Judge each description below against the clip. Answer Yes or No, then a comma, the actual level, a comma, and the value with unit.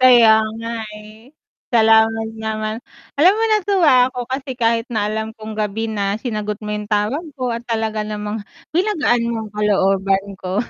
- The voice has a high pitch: Yes, high, 220 Hz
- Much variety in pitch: No, average, 2.7 semitones